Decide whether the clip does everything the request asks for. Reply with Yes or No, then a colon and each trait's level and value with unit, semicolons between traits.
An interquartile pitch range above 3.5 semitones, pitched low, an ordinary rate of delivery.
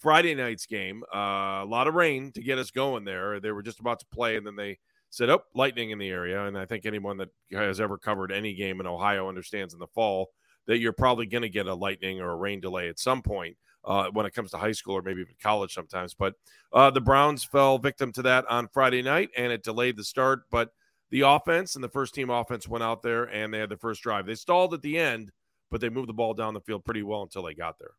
No: average, 4.3 semitones; low, 110 Hz; fast, 265 wpm